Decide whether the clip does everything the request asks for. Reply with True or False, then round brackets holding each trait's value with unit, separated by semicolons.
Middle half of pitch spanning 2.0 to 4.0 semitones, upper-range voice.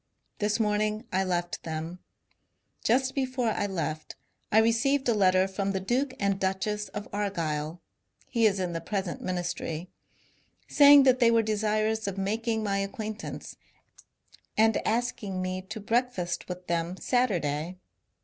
True (3.5 semitones; 205 Hz)